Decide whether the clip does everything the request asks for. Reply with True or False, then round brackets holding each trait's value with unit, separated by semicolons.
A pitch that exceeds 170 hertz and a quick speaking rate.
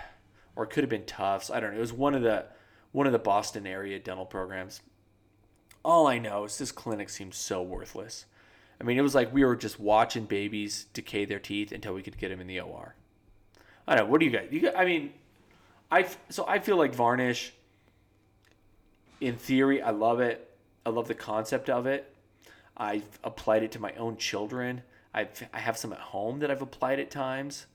False (110 Hz; 210 wpm)